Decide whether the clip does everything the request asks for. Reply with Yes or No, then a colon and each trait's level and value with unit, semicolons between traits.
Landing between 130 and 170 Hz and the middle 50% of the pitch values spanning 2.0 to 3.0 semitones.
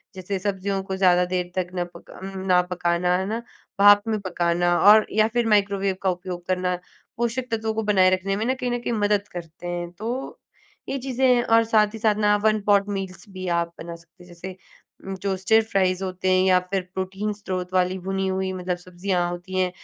No: high, 190 Hz; narrow, 2.4 semitones